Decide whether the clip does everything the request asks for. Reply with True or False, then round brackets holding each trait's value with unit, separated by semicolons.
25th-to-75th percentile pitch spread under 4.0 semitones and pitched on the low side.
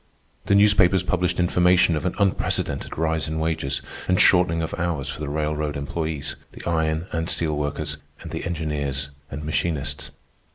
True (2.7 semitones; 80 Hz)